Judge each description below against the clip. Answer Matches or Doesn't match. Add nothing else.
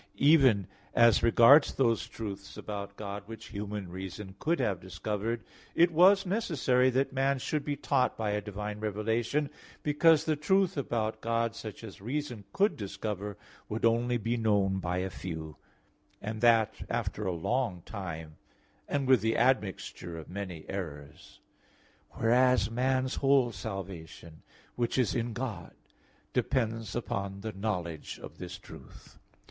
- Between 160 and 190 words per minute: Doesn't match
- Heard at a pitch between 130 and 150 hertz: Doesn't match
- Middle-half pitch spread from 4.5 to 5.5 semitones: Matches